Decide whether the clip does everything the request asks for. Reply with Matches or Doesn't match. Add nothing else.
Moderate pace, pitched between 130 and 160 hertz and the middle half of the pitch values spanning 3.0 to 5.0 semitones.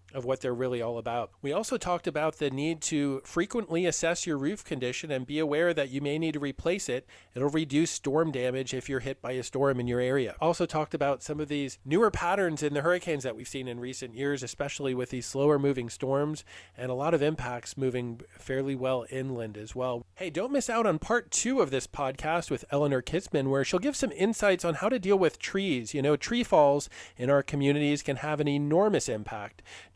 Doesn't match